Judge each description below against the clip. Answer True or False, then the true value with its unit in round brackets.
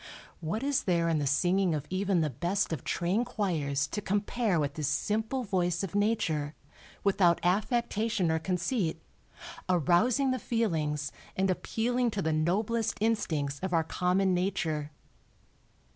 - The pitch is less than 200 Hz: True (185 Hz)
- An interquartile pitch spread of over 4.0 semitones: True (4.9 semitones)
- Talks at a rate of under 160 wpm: True (145 wpm)